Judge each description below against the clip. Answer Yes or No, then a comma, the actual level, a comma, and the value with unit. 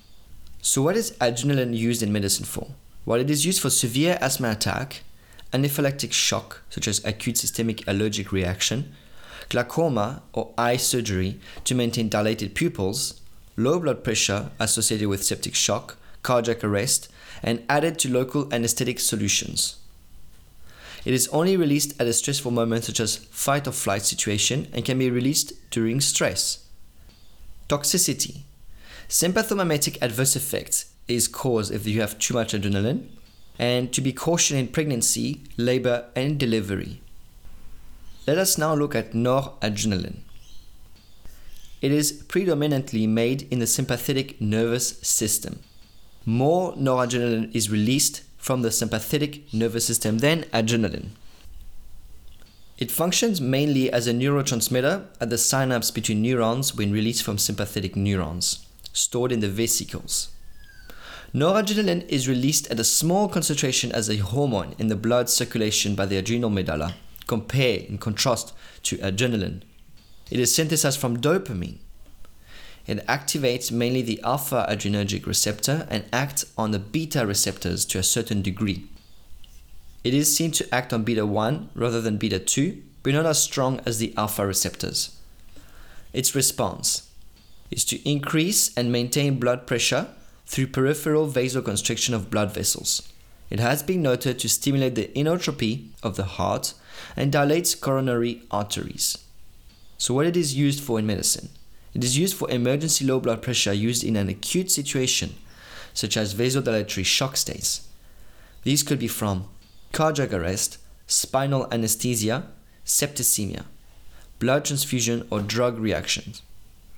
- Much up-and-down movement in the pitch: No, average, 4.8 semitones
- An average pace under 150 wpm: Yes, average, 140 wpm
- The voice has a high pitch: No, low, 115 Hz